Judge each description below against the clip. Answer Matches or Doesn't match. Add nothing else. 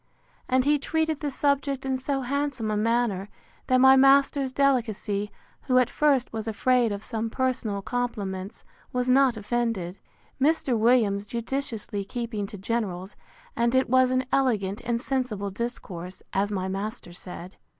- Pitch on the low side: Doesn't match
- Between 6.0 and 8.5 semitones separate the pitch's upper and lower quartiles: Doesn't match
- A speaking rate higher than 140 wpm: Matches